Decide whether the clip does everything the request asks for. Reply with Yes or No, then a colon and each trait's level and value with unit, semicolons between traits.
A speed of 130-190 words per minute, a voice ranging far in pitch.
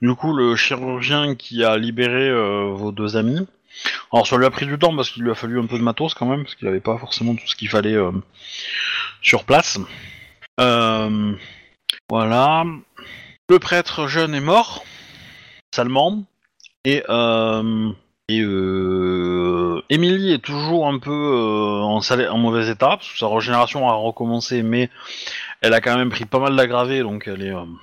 No: average, 180 wpm; average, 3.8 semitones